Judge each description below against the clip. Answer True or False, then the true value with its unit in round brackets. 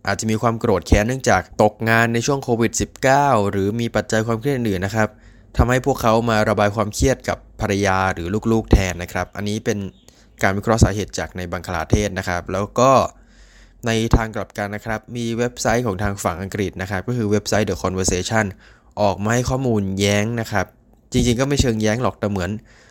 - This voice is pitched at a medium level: False (110 Hz)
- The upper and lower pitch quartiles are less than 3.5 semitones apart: True (2.8 semitones)